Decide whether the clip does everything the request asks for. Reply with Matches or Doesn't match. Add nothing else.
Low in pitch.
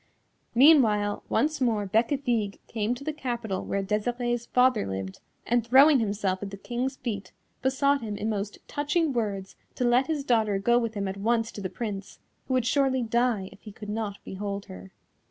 Doesn't match